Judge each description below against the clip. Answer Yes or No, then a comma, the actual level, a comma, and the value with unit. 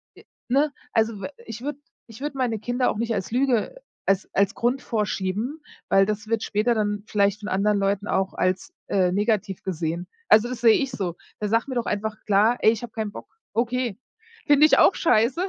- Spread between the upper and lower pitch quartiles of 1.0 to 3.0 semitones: No, average, 3.4 semitones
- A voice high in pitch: Yes, high, 220 Hz